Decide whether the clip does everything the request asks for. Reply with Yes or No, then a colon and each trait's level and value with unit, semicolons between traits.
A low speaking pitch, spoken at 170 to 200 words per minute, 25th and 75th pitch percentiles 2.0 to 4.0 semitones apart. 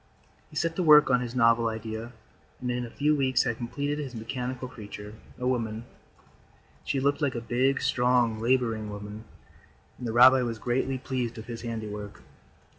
Yes: low, 120 Hz; average, 175 wpm; narrow, 2.5 semitones